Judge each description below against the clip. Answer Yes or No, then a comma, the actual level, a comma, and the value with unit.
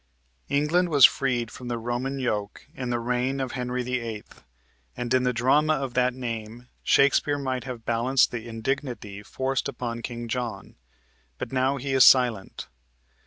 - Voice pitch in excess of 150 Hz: No, low, 125 Hz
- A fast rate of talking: No, average, 160 wpm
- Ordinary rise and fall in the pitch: No, narrow, 2.2 semitones